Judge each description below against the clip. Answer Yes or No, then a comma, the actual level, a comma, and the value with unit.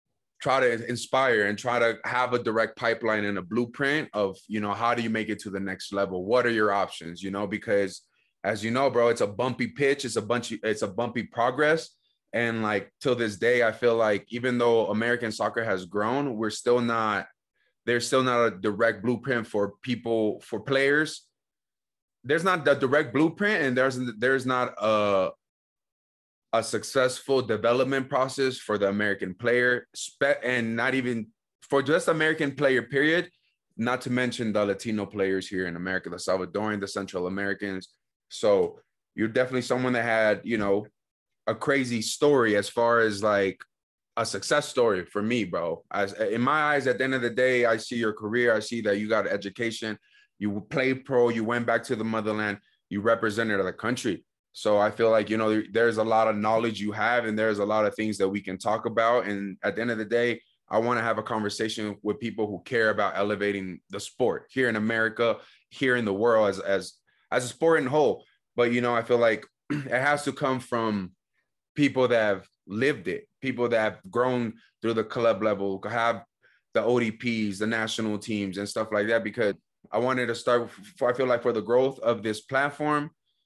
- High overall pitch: No, low, 115 Hz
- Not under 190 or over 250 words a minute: Yes, average, 200 wpm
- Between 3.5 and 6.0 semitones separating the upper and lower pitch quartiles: No, average, 3.0 semitones